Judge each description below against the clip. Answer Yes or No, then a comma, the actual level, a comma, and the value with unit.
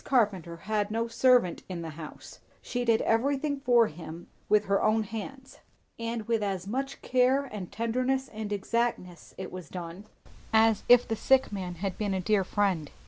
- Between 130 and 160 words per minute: No, average, 175 wpm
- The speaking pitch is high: Yes, high, 215 Hz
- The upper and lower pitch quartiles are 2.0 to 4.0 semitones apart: No, average, 4.4 semitones